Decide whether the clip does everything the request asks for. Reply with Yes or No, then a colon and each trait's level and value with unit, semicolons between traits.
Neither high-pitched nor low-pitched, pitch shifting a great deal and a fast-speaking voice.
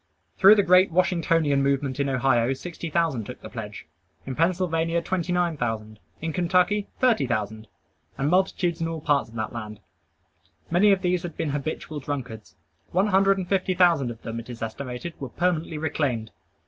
No: medium, 160 Hz; wide, 5.8 semitones; average, 175 wpm